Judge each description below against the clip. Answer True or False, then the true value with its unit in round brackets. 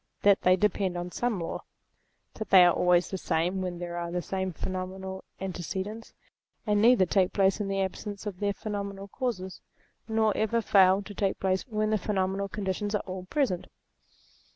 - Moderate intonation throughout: False (2.1 semitones)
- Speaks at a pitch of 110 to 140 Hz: False (195 Hz)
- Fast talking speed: False (175 wpm)